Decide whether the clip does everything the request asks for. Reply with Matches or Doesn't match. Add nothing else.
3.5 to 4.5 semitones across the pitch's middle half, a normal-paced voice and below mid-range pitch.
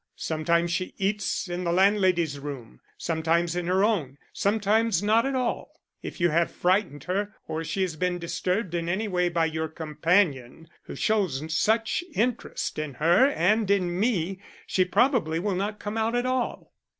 Doesn't match